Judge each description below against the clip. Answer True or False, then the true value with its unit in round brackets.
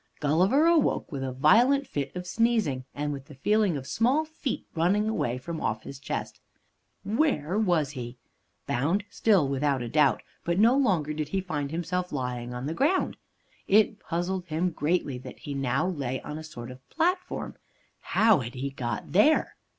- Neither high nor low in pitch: True (160 Hz)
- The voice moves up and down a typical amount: False (7.4 semitones)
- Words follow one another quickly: False (175 wpm)